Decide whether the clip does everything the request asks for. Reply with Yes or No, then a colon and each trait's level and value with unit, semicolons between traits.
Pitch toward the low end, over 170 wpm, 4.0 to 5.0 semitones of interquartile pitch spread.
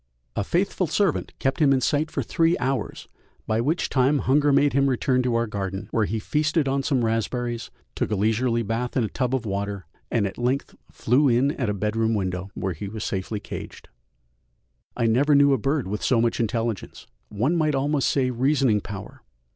Yes: low, 125 Hz; average, 195 wpm; average, 4.3 semitones